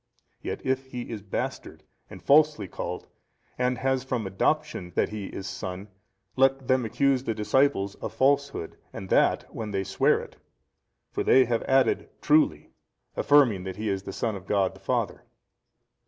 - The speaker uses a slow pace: No, average, 165 wpm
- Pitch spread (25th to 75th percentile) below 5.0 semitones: No, wide, 5.4 semitones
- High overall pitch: No, low, 115 Hz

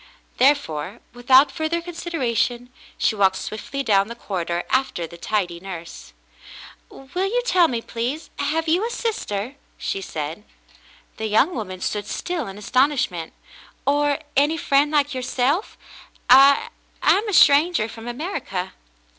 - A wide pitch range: Yes, wide, 6.5 semitones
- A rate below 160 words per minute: Yes, average, 150 wpm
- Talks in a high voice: Yes, very high, 255 Hz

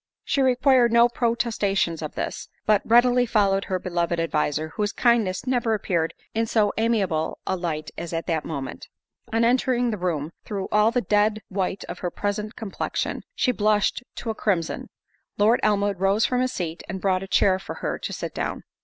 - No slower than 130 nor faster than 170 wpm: No, average, 185 wpm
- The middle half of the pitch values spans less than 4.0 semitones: No, average, 4.3 semitones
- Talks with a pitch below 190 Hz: No, high, 205 Hz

